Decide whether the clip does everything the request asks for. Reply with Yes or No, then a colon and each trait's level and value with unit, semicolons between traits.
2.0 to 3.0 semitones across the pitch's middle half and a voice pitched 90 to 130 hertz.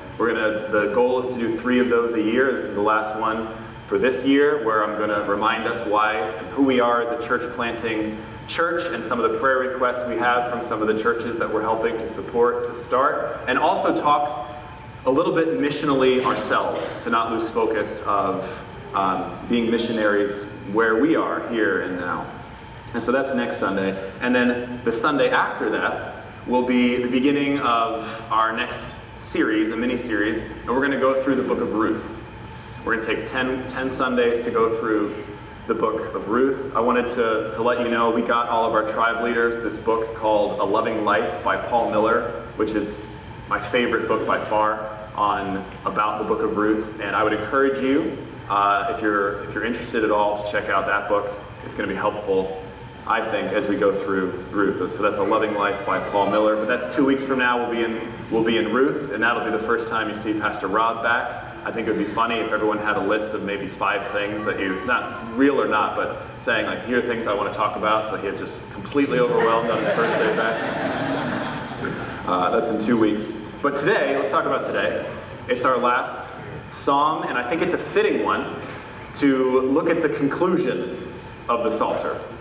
Yes: narrow, 2.5 semitones; low, 115 Hz